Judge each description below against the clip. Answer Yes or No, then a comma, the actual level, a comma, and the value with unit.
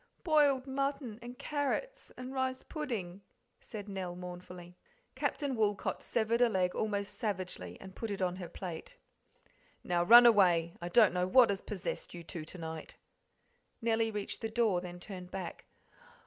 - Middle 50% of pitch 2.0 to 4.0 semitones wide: No, average, 5.1 semitones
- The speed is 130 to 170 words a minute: Yes, average, 160 wpm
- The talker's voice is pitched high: Yes, high, 200 Hz